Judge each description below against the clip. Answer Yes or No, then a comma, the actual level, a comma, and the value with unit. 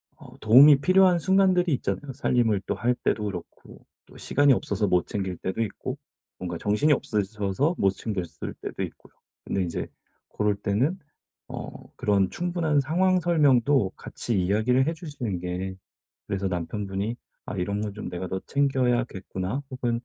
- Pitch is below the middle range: Yes, low, 110 Hz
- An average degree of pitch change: No, wide, 6.7 semitones